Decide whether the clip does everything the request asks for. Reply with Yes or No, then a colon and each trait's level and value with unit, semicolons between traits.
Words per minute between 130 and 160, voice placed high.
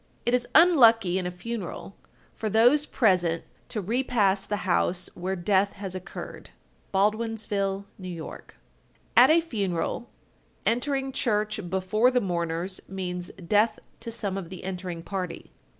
Yes: slow, 135 wpm; high, 200 Hz